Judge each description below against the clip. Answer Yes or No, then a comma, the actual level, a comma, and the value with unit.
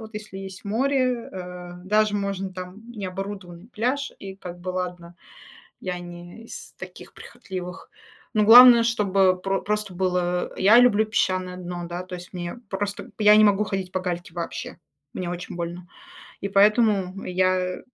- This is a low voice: No, high, 190 Hz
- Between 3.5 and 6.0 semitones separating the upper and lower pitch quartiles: No, average, 2.8 semitones